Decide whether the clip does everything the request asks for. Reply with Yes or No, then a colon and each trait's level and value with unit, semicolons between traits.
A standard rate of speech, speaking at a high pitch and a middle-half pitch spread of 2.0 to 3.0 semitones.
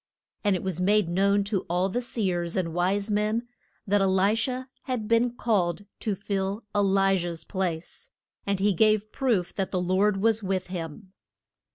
Yes: average, 180 wpm; high, 195 Hz; narrow, 2.5 semitones